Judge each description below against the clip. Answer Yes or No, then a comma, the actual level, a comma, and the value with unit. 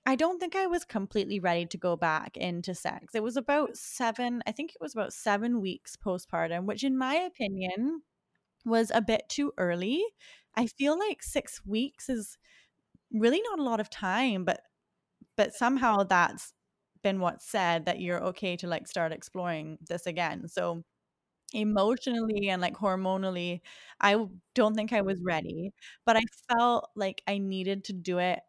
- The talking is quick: No, average, 170 wpm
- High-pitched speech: Yes, high, 210 Hz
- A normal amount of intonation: Yes, average, 4.9 semitones